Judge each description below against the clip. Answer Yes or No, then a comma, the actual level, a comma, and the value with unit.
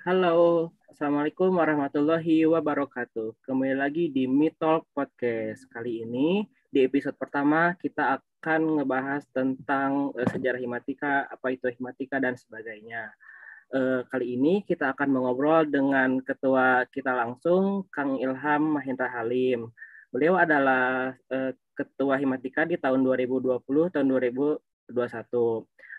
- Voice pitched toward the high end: No, low, 135 Hz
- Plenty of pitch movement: No, average, 2.8 semitones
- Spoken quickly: No, average, 120 wpm